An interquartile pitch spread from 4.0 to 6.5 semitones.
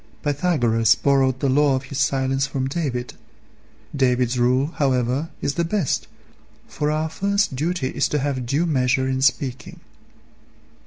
No: narrow, 2.5 semitones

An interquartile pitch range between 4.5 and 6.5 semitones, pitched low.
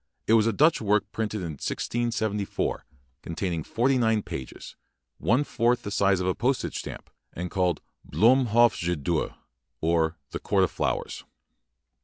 Yes: average, 5.1 semitones; low, 105 Hz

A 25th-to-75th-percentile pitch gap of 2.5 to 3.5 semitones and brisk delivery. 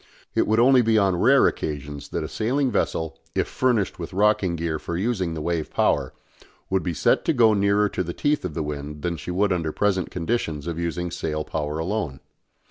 No: average, 4.9 semitones; fast, 210 wpm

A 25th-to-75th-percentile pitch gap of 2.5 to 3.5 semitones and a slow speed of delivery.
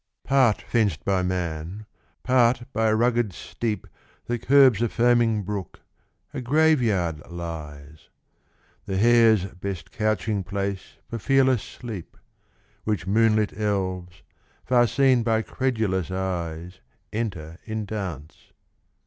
No: average, 4.4 semitones; slow, 120 wpm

